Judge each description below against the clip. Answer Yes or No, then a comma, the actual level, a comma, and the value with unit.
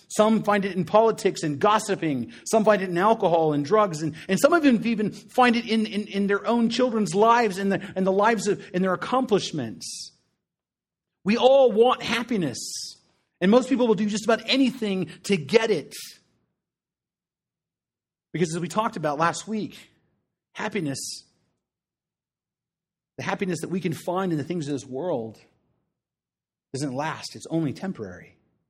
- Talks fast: No, average, 165 wpm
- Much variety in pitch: No, average, 4.2 semitones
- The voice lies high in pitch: Yes, high, 200 Hz